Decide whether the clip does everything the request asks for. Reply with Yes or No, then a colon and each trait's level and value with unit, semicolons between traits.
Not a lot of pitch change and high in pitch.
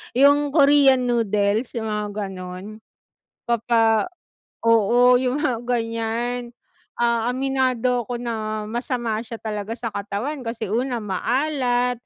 Yes: narrow, 2.3 semitones; high, 235 Hz